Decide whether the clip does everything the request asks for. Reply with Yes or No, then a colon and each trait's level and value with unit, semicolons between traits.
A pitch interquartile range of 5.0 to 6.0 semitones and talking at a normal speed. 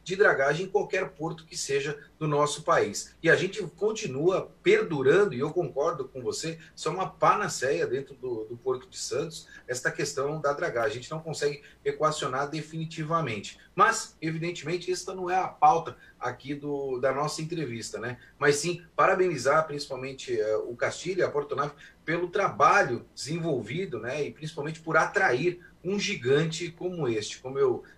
Yes: wide, 5.4 semitones; average, 165 wpm